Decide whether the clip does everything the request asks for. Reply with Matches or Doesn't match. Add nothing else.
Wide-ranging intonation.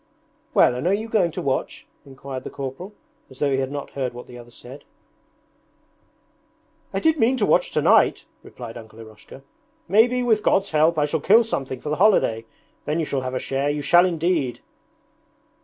Matches